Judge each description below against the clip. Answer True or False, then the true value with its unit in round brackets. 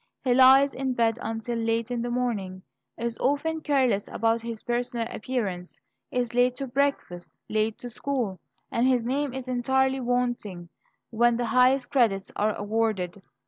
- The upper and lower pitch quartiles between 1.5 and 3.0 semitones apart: True (2.5 semitones)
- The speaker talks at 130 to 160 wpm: True (155 wpm)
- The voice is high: True (240 Hz)